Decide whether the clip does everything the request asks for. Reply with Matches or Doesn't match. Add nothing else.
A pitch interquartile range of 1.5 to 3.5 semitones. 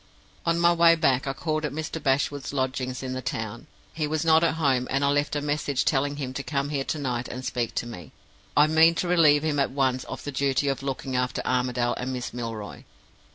Matches